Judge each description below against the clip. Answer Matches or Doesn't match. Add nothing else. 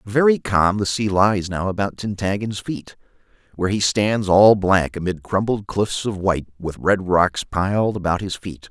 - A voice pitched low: Matches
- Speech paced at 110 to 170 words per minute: Doesn't match